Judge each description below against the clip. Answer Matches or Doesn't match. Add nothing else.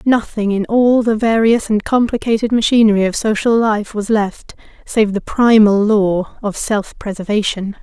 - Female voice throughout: Matches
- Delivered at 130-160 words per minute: Matches